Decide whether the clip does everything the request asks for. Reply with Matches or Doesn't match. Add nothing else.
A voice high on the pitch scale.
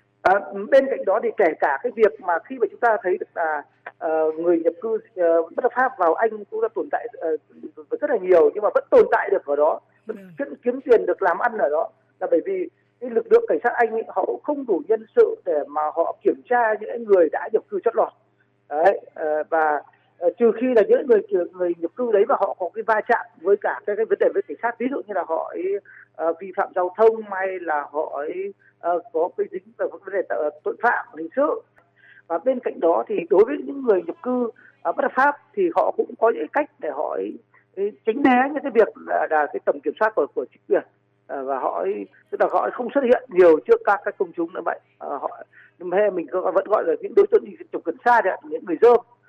Matches